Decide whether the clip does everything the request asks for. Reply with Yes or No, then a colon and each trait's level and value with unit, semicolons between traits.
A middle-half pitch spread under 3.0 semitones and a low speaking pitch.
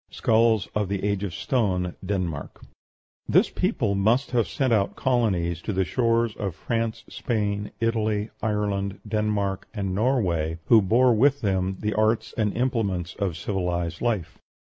No: average, 3.3 semitones; low, 105 Hz